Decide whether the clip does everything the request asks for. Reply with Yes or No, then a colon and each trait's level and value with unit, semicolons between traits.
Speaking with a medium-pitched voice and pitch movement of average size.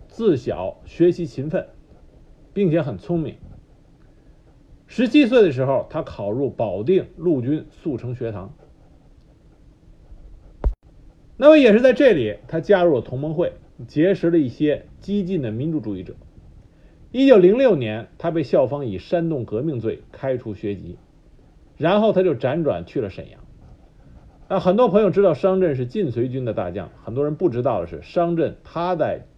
No: medium, 155 Hz; wide, 8.4 semitones